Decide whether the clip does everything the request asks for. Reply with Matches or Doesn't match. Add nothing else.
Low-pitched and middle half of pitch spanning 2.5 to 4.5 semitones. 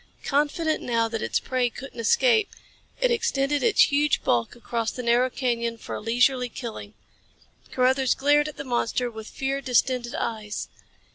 Doesn't match